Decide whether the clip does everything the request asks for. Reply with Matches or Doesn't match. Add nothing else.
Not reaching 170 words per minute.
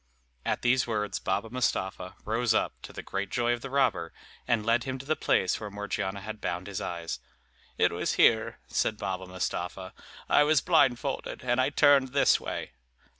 Doesn't match